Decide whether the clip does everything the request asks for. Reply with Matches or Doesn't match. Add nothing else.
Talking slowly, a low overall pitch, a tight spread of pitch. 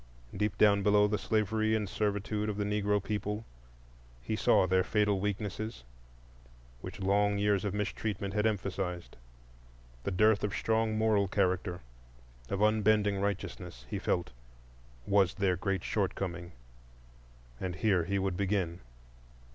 Matches